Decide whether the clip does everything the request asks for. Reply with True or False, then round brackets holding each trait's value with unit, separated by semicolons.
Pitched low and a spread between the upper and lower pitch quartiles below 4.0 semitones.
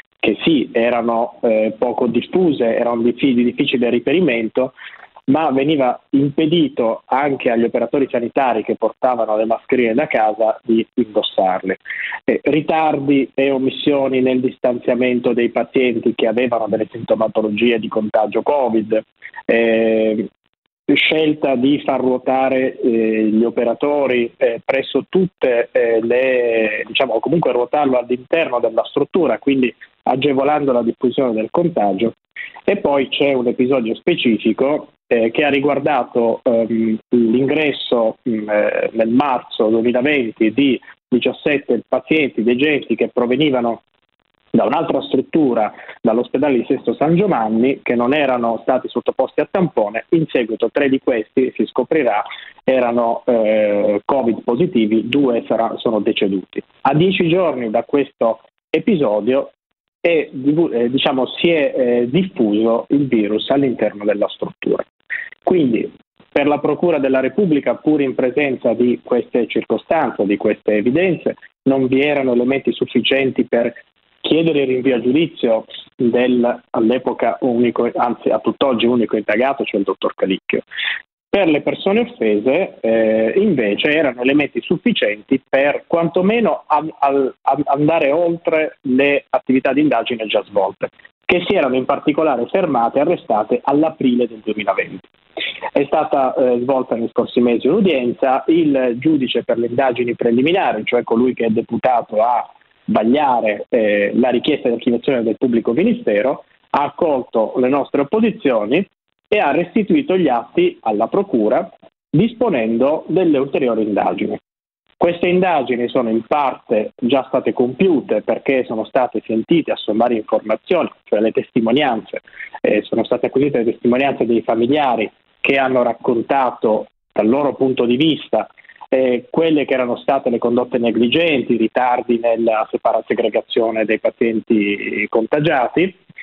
True (125 Hz; 3.4 semitones)